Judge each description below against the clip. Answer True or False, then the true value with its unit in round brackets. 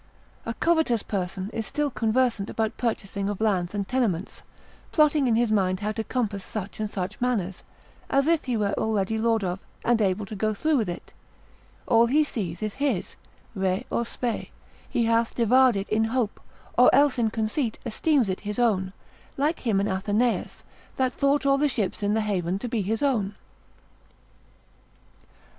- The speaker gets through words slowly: False (175 wpm)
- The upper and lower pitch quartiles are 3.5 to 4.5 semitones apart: True (3.9 semitones)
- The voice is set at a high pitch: True (220 Hz)